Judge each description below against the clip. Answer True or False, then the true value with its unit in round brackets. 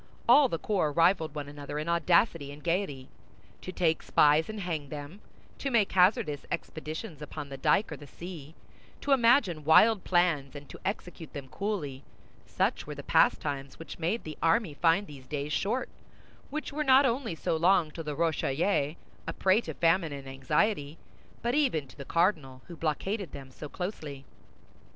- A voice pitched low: False (165 Hz)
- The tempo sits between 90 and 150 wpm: False (170 wpm)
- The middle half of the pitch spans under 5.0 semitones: False (5.3 semitones)